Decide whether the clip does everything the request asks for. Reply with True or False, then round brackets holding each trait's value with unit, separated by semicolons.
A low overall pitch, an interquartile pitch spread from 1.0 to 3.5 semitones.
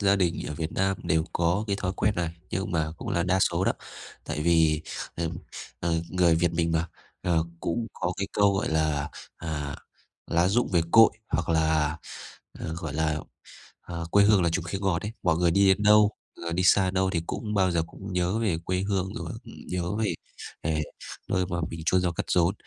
True (85 Hz; 2.8 semitones)